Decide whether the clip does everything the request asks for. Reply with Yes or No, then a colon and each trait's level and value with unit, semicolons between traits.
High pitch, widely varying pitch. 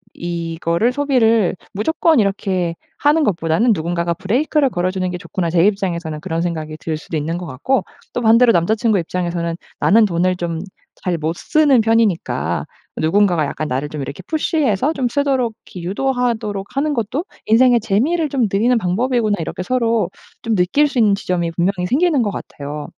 Yes: high, 200 Hz; wide, 6.3 semitones